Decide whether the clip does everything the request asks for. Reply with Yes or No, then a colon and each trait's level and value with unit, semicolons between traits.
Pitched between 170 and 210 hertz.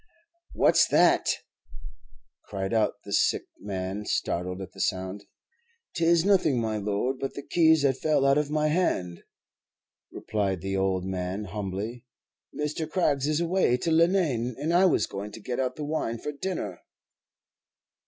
No: low, 125 Hz